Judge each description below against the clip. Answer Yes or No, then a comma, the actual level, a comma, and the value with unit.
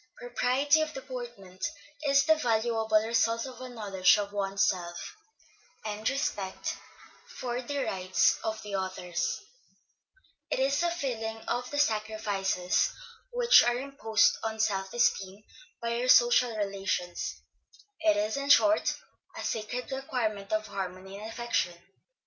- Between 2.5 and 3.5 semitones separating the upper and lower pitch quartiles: No, average, 4.3 semitones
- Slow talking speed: Yes, slow, 130 wpm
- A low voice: No, high, 225 Hz